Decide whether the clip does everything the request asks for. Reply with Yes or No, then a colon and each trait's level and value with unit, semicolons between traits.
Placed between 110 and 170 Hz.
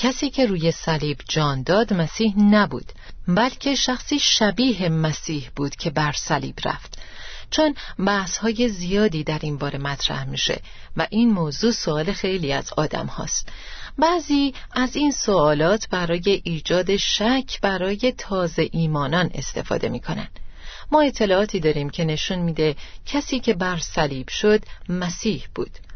No: high, 190 Hz